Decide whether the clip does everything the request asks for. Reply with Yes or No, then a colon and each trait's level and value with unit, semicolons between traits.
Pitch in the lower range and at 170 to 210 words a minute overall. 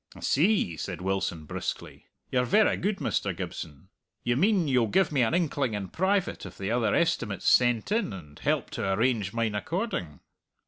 Yes: low, 120 Hz; average, 175 wpm